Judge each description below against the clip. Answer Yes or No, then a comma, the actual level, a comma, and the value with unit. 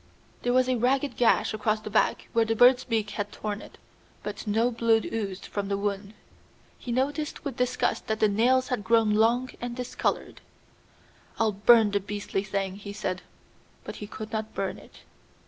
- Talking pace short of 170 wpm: No, average, 180 wpm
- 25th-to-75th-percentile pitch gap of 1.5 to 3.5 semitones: Yes, average, 3.0 semitones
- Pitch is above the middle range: Yes, high, 220 Hz